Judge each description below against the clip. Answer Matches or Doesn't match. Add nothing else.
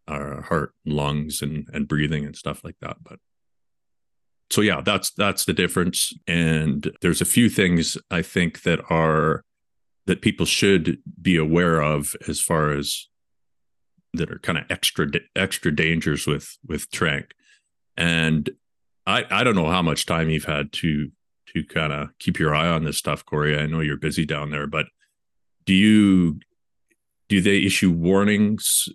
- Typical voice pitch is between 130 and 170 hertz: Doesn't match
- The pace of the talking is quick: Doesn't match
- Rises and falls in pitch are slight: Matches